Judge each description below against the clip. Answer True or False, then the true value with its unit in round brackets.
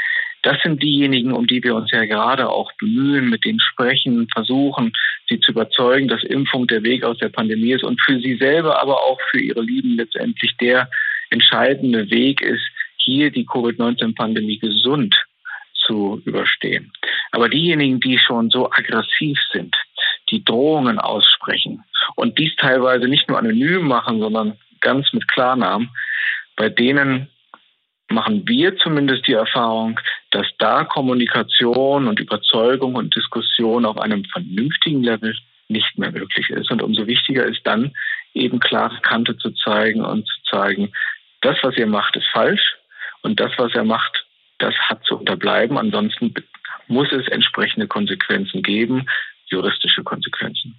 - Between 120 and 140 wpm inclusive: False (150 wpm)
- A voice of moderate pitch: False (130 Hz)